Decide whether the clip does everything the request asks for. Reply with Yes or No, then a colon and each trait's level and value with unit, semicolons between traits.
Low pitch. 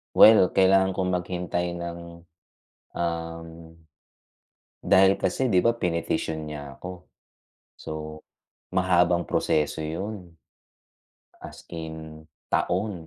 Yes: very low, 85 Hz